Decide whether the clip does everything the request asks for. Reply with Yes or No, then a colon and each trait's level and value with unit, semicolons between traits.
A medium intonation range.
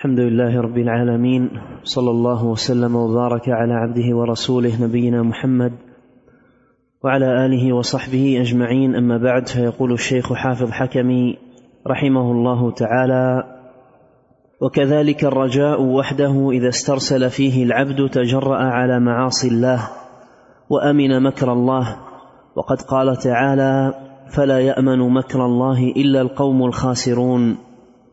No: narrow, 1.4 semitones